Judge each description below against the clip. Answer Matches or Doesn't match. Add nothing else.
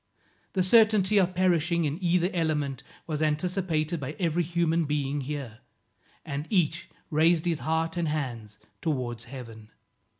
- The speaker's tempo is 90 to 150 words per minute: Matches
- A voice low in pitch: Doesn't match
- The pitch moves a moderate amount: Matches